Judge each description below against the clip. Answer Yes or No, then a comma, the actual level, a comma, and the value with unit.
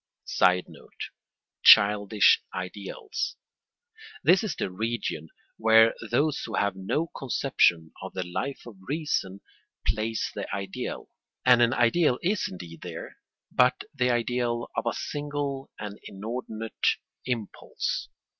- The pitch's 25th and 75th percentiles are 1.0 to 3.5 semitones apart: No, average, 4.9 semitones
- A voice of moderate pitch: No, low, 115 Hz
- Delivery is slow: Yes, slow, 115 wpm